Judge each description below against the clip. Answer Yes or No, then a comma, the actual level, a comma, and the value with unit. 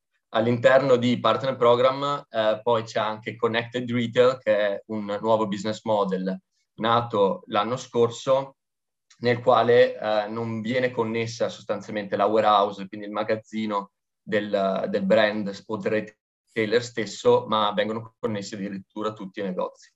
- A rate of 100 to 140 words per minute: Yes, average, 130 wpm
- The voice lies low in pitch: Yes, low, 110 Hz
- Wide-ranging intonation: No, narrow, 2.6 semitones